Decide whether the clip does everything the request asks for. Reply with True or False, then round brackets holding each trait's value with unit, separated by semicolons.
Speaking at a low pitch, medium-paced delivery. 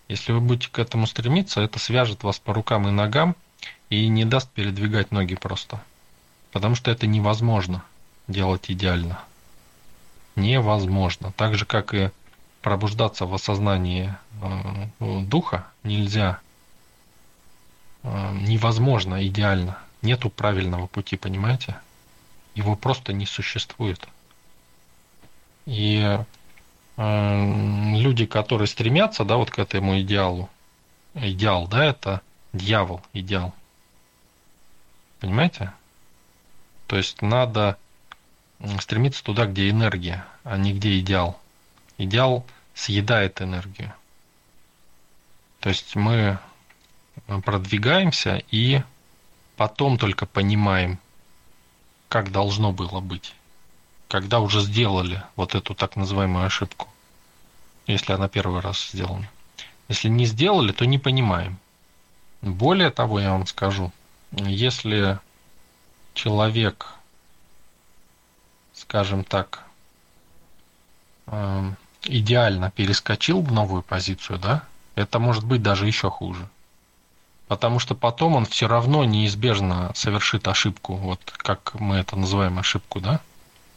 False (100 Hz; 100 wpm)